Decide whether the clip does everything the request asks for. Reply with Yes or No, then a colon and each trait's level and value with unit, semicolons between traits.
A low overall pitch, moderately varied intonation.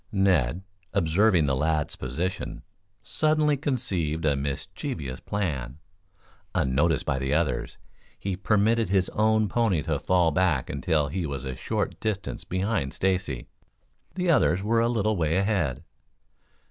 No: very low, 90 Hz; wide, 6.5 semitones